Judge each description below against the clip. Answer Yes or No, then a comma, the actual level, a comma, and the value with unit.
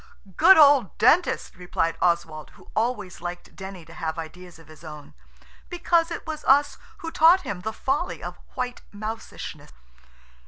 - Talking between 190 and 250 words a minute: No, average, 155 wpm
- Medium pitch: No, high, 205 Hz